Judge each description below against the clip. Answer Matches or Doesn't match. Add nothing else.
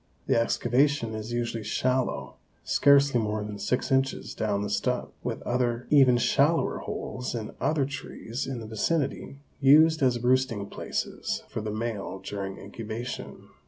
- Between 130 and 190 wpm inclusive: Matches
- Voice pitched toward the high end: Doesn't match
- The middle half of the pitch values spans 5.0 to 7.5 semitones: Doesn't match